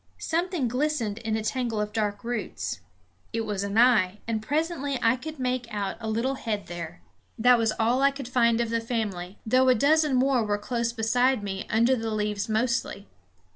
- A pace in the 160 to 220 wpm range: Yes, average, 190 wpm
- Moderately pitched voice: No, high, 230 Hz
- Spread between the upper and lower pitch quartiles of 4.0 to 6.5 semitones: No, average, 3.3 semitones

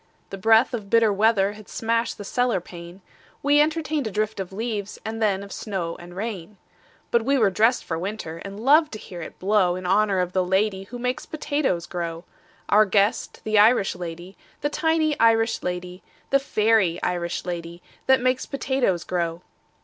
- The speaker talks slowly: No, average, 180 wpm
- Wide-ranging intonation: No, average, 4.3 semitones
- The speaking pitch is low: No, high, 210 Hz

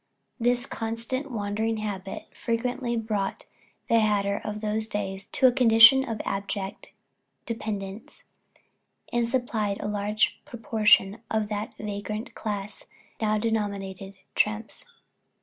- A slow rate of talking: Yes, slow, 115 wpm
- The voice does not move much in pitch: Yes, narrow, 2.1 semitones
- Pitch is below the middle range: No, high, 215 Hz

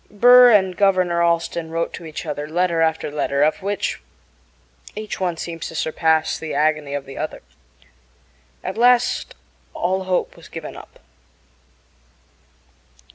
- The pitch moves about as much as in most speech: Yes, average, 3.3 semitones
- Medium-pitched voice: Yes, medium, 170 Hz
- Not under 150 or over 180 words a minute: No, slow, 135 wpm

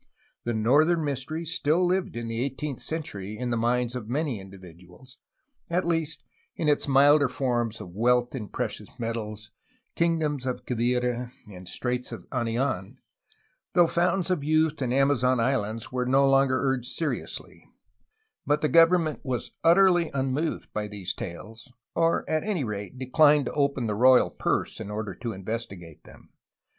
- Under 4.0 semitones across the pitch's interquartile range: No, average, 5.0 semitones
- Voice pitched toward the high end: No, low, 130 Hz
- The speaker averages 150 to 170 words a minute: Yes, average, 160 wpm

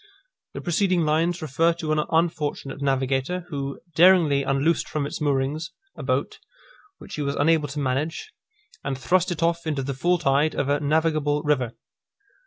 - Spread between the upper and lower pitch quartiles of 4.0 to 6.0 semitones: No, average, 3.0 semitones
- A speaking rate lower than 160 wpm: No, average, 165 wpm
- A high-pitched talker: No, medium, 150 Hz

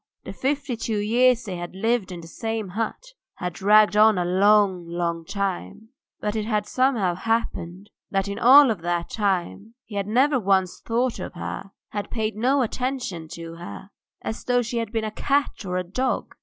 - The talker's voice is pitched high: Yes, high, 210 Hz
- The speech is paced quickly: No, average, 185 wpm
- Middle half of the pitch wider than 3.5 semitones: Yes, average, 4.3 semitones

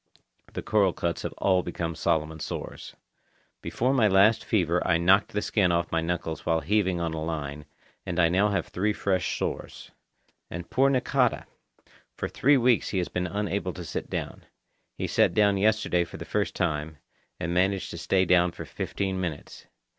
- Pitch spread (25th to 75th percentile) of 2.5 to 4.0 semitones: Yes, average, 3.4 semitones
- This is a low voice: Yes, very low, 90 Hz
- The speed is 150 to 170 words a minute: No, average, 180 wpm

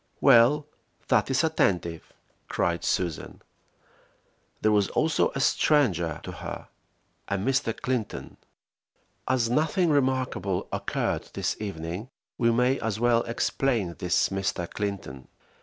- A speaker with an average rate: No, slow, 115 wpm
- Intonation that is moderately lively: No, wide, 5.9 semitones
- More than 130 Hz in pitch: No, low, 115 Hz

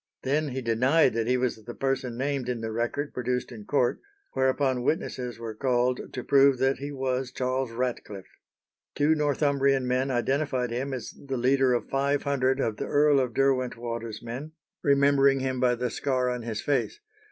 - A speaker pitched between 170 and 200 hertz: No, low, 130 Hz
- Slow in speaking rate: No, average, 175 wpm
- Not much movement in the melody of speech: Yes, narrow, 2.1 semitones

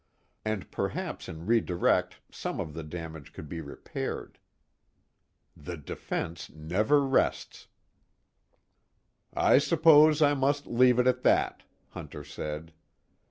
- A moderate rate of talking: No, slow, 115 wpm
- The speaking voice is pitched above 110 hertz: No, very low, 90 Hz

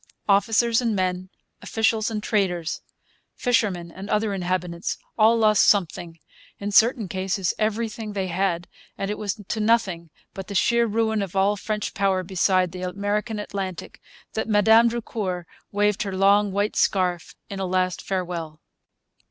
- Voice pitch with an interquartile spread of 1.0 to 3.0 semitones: Yes, average, 2.7 semitones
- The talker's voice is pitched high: Yes, high, 200 Hz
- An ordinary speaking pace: Yes, average, 150 wpm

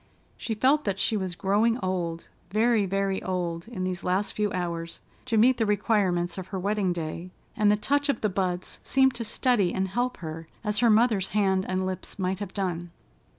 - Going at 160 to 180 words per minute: No, average, 195 wpm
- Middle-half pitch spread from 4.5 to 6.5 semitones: No, average, 3.2 semitones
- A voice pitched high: Yes, high, 195 Hz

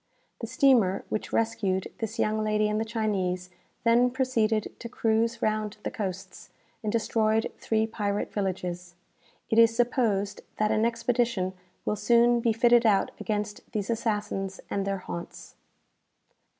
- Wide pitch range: No, narrow, 2.5 semitones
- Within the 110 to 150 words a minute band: Yes, average, 140 wpm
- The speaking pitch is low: No, high, 215 Hz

